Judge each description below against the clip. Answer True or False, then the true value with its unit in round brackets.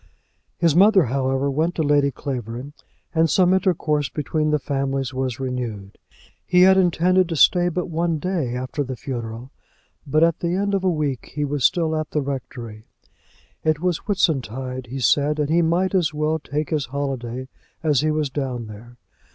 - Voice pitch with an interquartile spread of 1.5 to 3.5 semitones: False (4.3 semitones)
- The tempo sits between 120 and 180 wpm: True (175 wpm)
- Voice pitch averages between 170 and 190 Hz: False (145 Hz)